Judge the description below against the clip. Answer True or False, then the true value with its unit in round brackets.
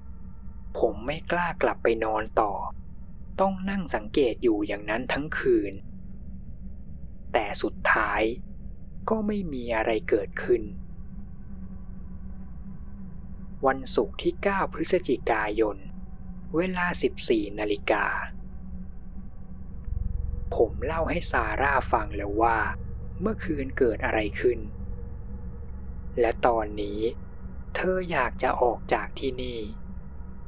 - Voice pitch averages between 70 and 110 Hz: True (105 Hz)